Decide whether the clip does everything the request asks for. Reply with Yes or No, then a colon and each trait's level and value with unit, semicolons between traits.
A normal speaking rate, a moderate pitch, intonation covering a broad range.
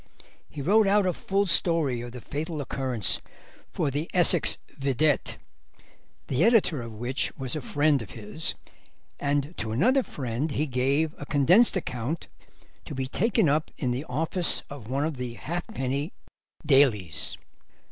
No: average, 150 wpm; medium, 145 Hz; average, 4.4 semitones